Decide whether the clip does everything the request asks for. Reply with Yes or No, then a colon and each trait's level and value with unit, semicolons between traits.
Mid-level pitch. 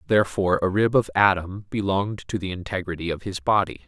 No: very low, 95 Hz